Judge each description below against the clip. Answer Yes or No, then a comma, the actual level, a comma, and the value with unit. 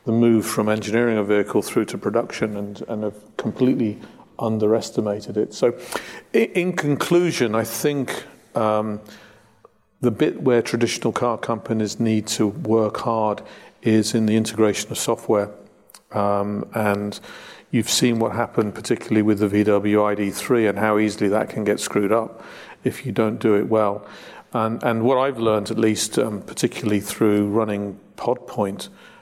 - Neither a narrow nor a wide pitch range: No, narrow, 1.7 semitones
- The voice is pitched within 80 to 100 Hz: No, low, 110 Hz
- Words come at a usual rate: Yes, average, 150 wpm